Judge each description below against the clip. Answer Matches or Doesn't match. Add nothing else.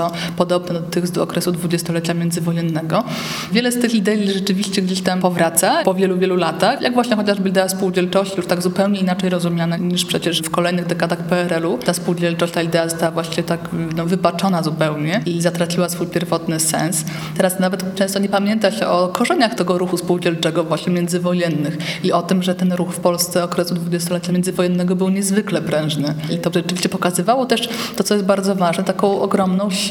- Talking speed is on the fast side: Matches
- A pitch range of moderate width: Doesn't match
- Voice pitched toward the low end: Doesn't match